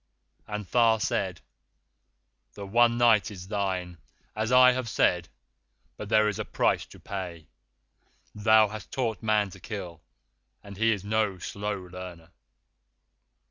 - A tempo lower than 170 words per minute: Yes, average, 140 wpm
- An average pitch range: Yes, average, 3.0 semitones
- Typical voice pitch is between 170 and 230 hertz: No, low, 105 Hz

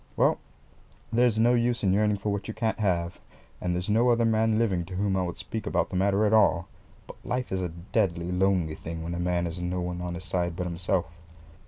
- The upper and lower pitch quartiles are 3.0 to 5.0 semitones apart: Yes, average, 3.7 semitones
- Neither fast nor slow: No, fast, 225 wpm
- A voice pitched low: Yes, very low, 95 Hz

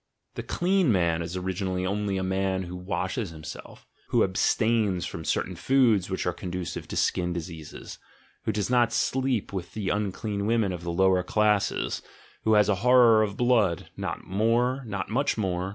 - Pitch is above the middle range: No, low, 100 Hz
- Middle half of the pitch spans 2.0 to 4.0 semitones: Yes, average, 3.5 semitones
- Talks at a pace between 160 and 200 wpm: Yes, average, 175 wpm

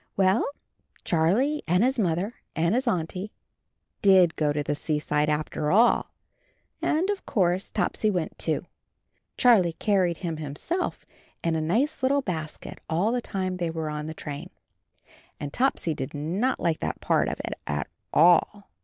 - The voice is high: No, medium, 175 Hz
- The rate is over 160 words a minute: No, average, 155 wpm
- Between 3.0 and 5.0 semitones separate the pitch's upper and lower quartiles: No, wide, 5.6 semitones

